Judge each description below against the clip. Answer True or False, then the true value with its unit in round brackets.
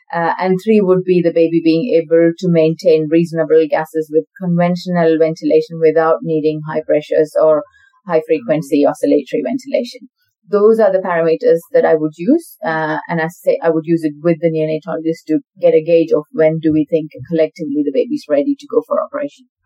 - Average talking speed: True (185 wpm)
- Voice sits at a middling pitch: True (165 Hz)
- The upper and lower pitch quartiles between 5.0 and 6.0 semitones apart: True (5.6 semitones)